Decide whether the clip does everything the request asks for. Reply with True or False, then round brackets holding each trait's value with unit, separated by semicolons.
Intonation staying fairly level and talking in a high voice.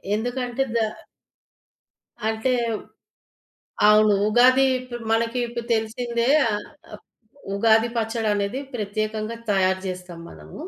True (2.3 semitones; 225 Hz)